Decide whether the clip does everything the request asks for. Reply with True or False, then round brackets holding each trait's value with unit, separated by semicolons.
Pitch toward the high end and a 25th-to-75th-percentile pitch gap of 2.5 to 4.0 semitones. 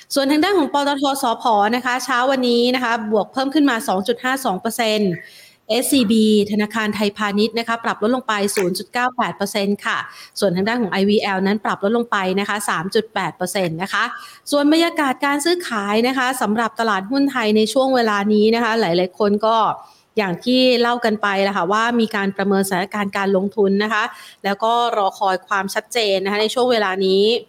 True (220 Hz; 3.4 semitones)